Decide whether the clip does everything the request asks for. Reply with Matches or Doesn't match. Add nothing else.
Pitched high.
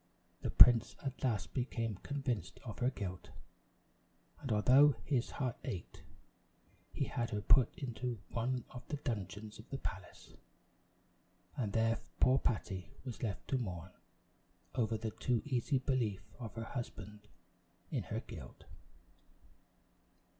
Doesn't match